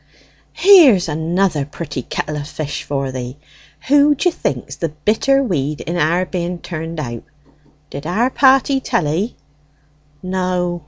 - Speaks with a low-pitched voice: No, medium, 175 Hz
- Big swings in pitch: Yes, wide, 6.2 semitones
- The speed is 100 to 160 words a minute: Yes, average, 140 wpm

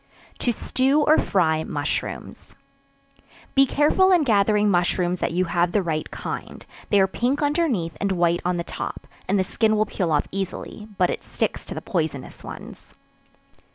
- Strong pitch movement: Yes, wide, 5.8 semitones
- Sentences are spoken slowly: No, average, 170 wpm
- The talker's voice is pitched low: No, high, 195 Hz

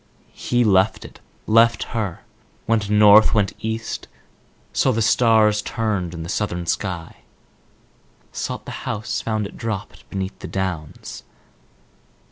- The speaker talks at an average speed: No, slow, 125 wpm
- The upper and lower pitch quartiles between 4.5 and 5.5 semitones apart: No, average, 2.7 semitones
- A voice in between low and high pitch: No, low, 105 Hz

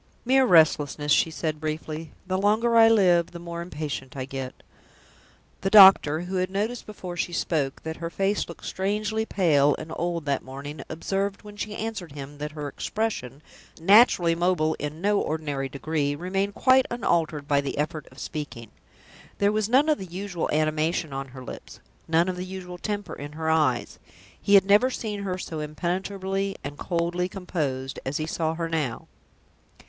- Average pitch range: Yes, average, 4.7 semitones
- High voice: No, medium, 170 Hz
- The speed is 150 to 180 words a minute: Yes, average, 175 wpm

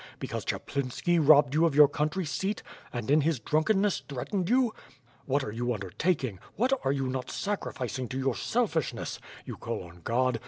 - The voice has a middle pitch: Yes, medium, 145 Hz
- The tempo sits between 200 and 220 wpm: No, average, 180 wpm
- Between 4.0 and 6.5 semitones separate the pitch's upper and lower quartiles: Yes, wide, 5.4 semitones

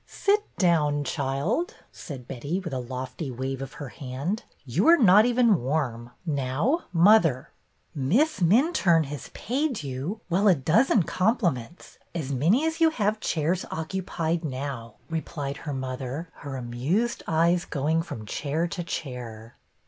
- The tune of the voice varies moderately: No, wide, 6.6 semitones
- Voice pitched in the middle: Yes, medium, 160 Hz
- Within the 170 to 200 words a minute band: No, average, 150 wpm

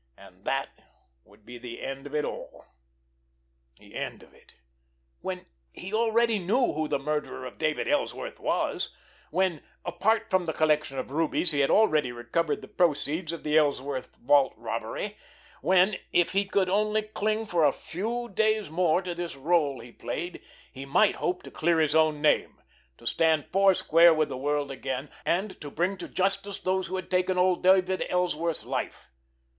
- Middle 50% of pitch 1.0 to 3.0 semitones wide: No, average, 4.6 semitones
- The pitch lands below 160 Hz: No, medium, 170 Hz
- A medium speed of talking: Yes, average, 170 wpm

